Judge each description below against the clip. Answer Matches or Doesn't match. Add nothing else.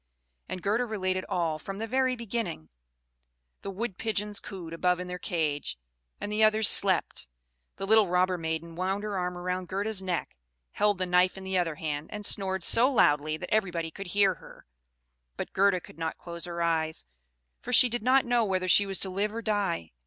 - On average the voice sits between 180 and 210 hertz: Matches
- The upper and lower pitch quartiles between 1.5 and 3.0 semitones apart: Doesn't match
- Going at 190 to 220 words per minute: Matches